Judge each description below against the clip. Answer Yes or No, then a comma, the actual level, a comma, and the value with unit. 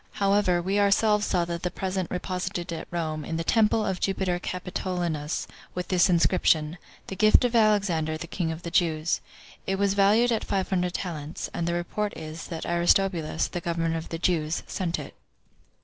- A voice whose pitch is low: No, medium, 180 Hz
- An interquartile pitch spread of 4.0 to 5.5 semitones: No, average, 2.9 semitones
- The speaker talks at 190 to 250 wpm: No, average, 180 wpm